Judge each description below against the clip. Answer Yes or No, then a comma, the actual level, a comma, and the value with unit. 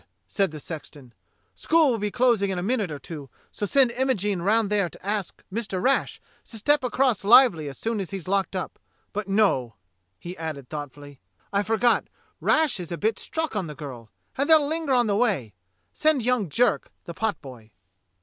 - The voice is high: Yes, high, 200 Hz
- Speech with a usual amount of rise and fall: No, wide, 7.1 semitones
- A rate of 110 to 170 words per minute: No, average, 195 wpm